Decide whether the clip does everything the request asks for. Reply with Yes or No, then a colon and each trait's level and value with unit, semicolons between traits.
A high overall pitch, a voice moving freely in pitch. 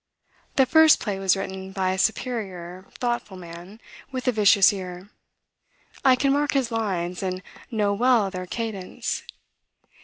No: high, 200 Hz; average, 4.4 semitones